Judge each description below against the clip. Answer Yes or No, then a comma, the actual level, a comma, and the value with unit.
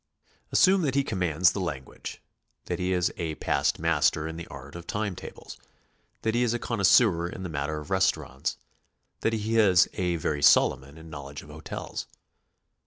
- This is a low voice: Yes, very low, 90 Hz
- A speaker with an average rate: Yes, average, 180 wpm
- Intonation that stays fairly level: No, average, 5.3 semitones